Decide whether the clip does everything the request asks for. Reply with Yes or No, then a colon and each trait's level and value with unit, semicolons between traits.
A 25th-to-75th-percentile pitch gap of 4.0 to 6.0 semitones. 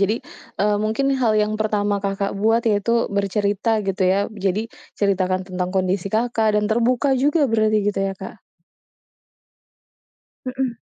No: narrow, 2.5 semitones